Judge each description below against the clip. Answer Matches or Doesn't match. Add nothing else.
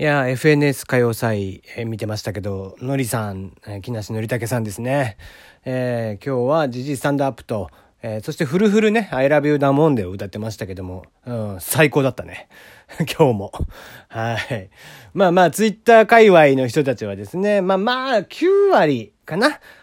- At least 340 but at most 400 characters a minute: Matches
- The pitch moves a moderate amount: Doesn't match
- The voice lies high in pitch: Doesn't match